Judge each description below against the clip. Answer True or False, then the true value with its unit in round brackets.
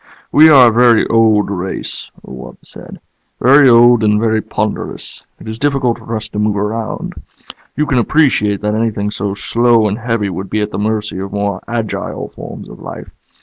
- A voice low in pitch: True (110 Hz)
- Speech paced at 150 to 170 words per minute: False (190 wpm)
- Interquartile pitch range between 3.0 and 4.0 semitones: False (2.4 semitones)